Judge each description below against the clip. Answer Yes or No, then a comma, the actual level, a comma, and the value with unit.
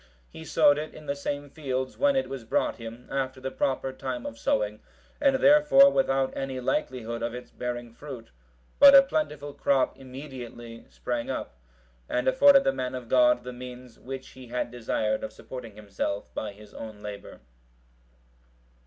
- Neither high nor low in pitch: No, low, 130 Hz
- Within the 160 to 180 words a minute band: Yes, average, 170 wpm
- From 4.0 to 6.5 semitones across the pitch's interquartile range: No, average, 3.4 semitones